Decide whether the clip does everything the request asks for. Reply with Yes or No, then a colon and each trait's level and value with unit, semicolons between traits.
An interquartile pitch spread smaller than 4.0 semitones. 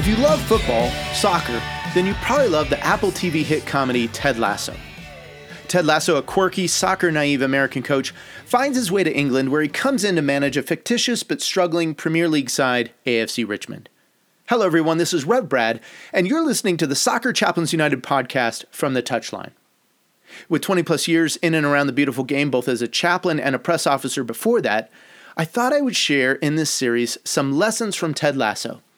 No: average, 5.1 semitones